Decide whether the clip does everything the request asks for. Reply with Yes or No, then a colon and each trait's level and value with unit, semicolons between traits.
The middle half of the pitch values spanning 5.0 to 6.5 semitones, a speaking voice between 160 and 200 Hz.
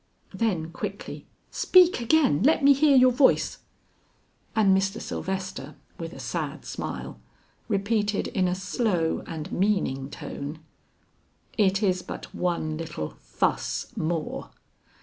Yes: wide, 5.6 semitones; high, 190 Hz